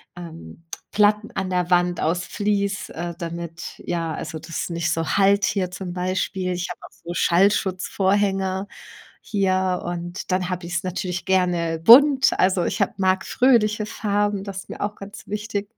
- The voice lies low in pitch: No, medium, 185 Hz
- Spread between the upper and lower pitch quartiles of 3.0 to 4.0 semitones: No, narrow, 2.5 semitones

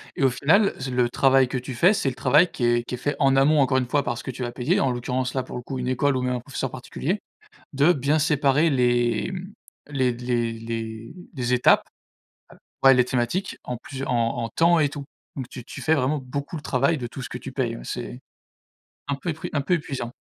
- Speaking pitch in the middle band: No, low, 130 Hz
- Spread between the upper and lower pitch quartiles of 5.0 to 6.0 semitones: No, average, 2.8 semitones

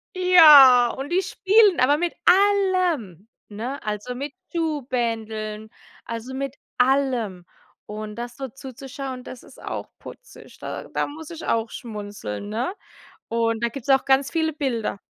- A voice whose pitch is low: No, very high, 260 Hz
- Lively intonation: No, average, 5.0 semitones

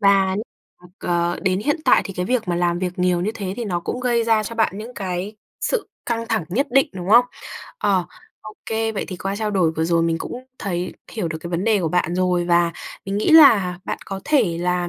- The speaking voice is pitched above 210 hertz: No, high, 190 Hz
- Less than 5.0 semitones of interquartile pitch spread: Yes, average, 4.1 semitones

